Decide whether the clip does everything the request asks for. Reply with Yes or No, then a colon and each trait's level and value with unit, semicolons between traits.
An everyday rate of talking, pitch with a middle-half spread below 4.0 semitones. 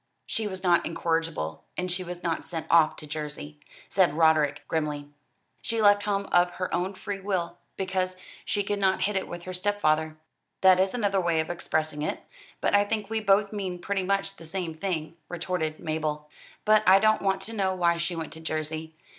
Yes: average, 195 wpm; average, 3.6 semitones